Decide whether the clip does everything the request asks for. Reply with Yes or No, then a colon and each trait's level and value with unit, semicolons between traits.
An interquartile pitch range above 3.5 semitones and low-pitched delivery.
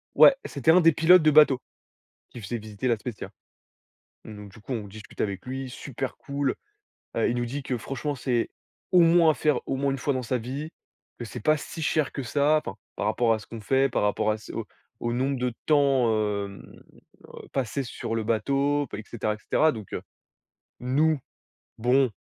Yes: average, 4.1 semitones; low, 130 Hz